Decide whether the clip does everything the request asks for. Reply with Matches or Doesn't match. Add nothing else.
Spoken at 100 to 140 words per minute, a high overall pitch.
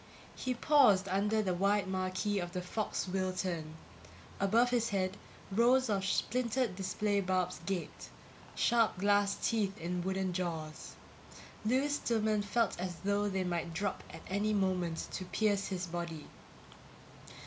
Matches